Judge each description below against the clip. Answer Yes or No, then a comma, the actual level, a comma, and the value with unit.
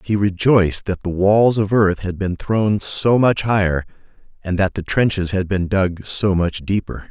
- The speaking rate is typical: Yes, average, 195 wpm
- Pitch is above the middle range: No, low, 100 Hz